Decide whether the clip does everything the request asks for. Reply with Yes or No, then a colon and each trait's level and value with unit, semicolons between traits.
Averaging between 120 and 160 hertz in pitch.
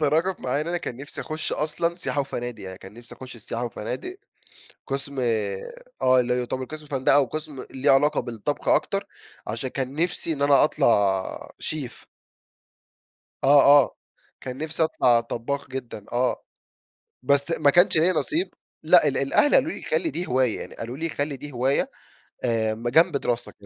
Yes: low, 135 Hz